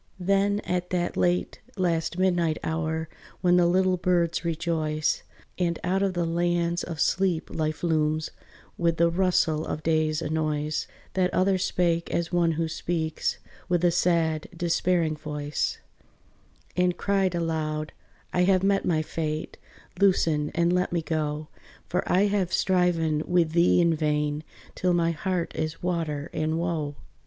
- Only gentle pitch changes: Yes, narrow, 2.2 semitones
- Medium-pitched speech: Yes, medium, 170 Hz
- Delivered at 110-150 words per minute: Yes, average, 145 wpm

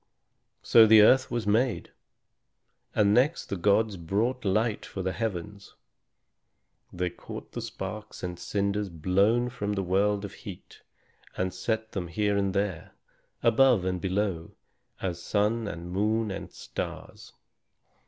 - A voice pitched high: No, low, 100 Hz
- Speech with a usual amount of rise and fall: Yes, average, 3.0 semitones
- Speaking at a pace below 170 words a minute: Yes, slow, 135 wpm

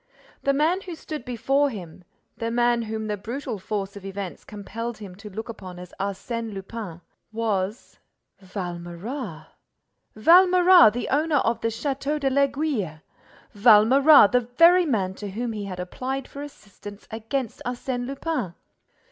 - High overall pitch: Yes, high, 230 Hz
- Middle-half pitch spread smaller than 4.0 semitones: No, wide, 5.5 semitones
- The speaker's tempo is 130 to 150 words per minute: Yes, average, 140 wpm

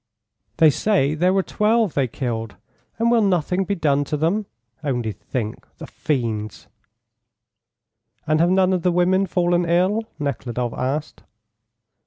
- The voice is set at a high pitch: No, medium, 165 Hz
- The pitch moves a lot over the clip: Yes, wide, 6.1 semitones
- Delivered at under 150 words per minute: Yes, average, 140 wpm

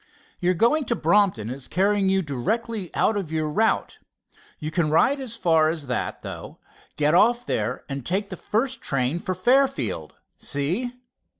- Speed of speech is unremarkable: Yes, average, 165 wpm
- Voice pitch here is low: No, medium, 185 Hz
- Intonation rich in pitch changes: Yes, wide, 6.9 semitones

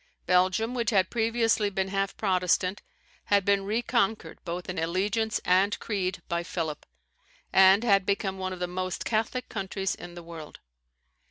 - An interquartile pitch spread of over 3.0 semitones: No, average, 2.7 semitones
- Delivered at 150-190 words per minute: Yes, average, 155 wpm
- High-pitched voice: Yes, high, 195 Hz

